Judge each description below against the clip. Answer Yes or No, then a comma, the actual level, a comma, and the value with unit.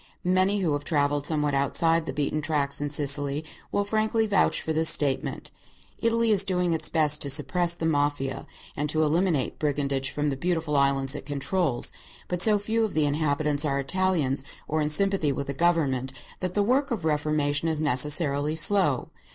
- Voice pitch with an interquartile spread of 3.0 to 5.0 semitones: Yes, average, 3.9 semitones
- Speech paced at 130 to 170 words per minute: No, average, 180 wpm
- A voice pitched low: No, medium, 150 Hz